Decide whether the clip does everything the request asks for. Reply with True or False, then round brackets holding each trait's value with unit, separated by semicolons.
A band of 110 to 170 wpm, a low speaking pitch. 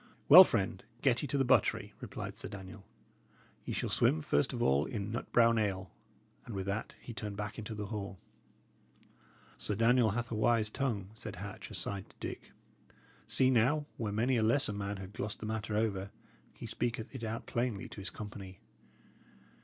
False (185 wpm; 110 Hz)